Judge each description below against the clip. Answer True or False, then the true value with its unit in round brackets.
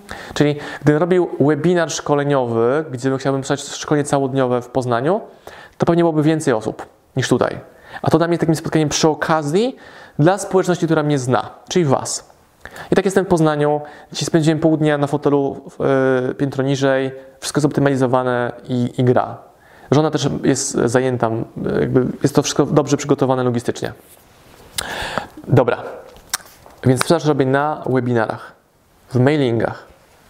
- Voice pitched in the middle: True (145 Hz)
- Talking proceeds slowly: False (145 wpm)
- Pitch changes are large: False (3.2 semitones)